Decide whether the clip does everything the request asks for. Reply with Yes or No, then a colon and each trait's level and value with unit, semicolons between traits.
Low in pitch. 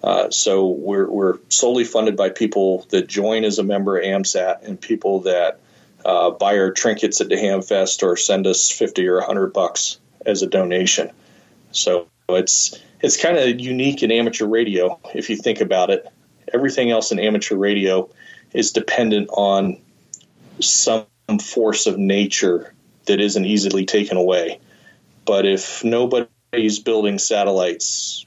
Yes: low, 100 Hz